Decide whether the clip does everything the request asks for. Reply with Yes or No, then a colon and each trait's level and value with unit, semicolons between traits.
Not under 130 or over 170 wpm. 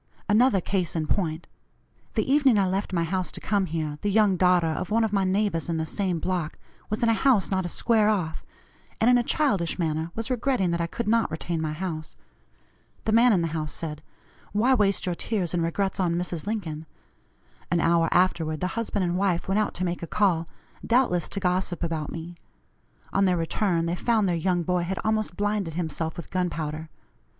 No: fast, 205 wpm